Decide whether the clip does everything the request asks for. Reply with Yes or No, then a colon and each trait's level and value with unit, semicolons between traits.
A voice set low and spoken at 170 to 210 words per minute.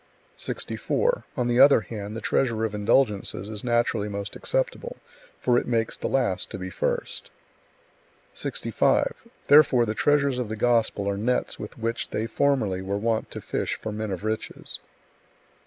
No: low, 115 Hz; average, 160 wpm